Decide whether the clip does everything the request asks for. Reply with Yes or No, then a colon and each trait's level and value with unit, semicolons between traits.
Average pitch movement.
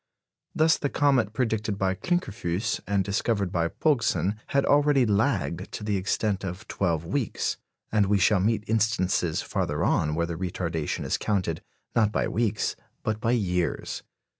Yes: average, 3.7 semitones